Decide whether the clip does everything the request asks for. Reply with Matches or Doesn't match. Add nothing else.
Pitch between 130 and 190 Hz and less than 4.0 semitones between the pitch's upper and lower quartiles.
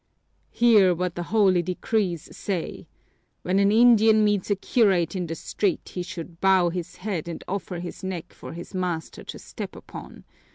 Matches